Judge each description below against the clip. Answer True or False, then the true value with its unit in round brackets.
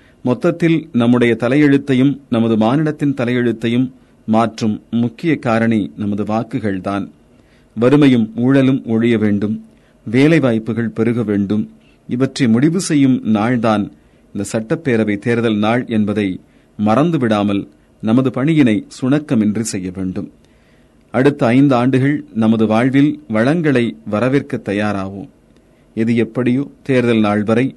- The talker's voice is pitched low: True (115 Hz)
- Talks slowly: False (100 wpm)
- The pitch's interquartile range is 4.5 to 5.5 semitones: False (3.8 semitones)